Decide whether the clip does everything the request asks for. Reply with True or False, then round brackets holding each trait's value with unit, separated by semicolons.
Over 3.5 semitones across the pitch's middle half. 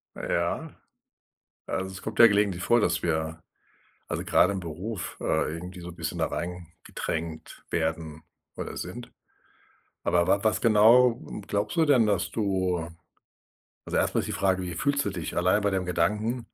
True (4.0 semitones)